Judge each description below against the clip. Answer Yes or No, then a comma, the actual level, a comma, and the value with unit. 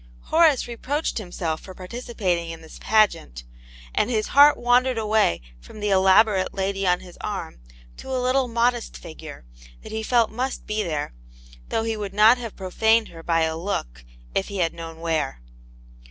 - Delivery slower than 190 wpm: Yes, average, 175 wpm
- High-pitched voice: Yes, high, 205 Hz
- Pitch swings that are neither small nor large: No, wide, 5.8 semitones